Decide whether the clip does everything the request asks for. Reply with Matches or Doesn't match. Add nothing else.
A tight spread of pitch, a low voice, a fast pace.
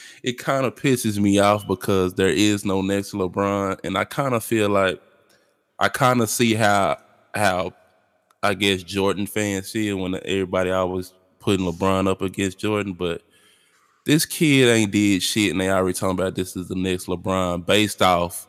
Doesn't match